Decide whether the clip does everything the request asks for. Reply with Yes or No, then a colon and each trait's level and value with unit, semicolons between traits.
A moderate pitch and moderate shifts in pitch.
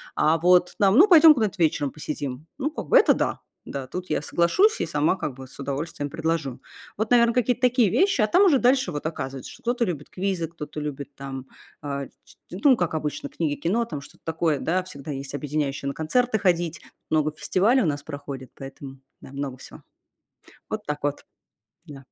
No: medium, 160 Hz; wide, 6.9 semitones